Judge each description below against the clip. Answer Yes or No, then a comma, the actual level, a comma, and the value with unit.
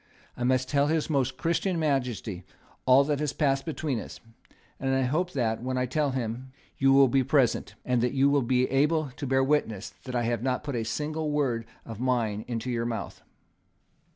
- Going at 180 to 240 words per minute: Yes, average, 195 wpm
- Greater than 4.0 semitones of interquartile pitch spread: No, average, 3.0 semitones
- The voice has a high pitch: No, low, 130 Hz